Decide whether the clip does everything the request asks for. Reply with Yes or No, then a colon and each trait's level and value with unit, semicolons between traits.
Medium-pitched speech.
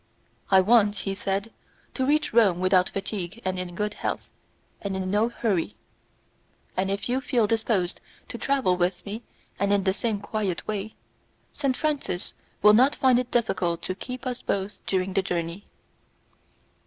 No: high, 200 Hz